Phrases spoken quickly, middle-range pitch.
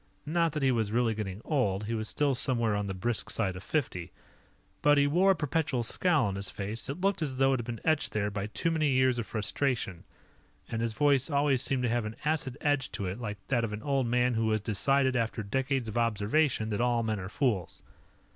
No: fast, 230 wpm; low, 120 Hz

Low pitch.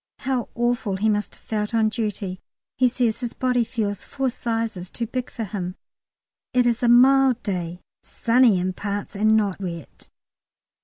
No: high, 225 Hz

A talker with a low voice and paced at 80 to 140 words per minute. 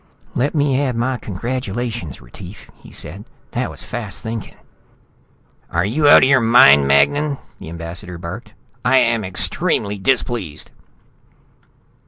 Yes: low, 110 Hz; slow, 135 wpm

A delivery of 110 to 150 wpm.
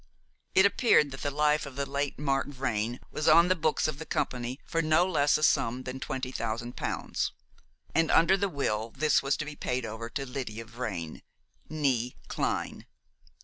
No: average, 185 wpm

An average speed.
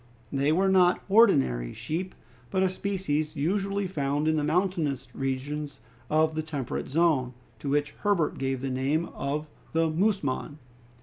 Yes: average, 145 wpm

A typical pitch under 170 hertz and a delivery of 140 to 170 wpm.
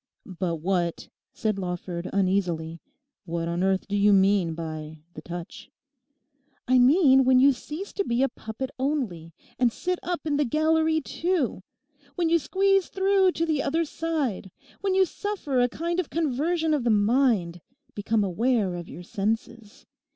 No: high, 245 Hz; average, 160 wpm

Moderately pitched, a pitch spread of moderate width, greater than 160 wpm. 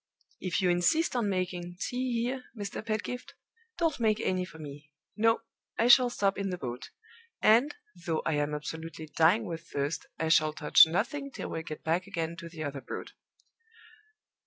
No: medium, 180 Hz; wide, 6.0 semitones; average, 175 wpm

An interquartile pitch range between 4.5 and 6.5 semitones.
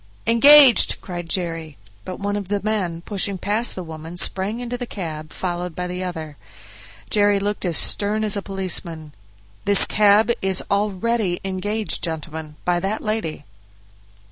No: average, 3.4 semitones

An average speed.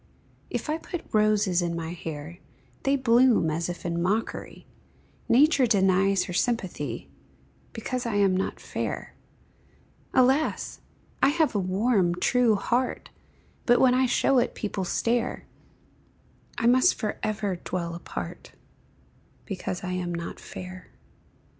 No: slow, 130 wpm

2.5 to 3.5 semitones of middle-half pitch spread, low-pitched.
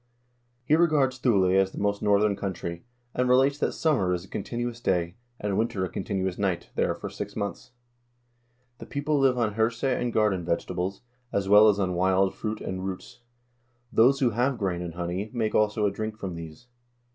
No: average, 4.2 semitones; low, 105 Hz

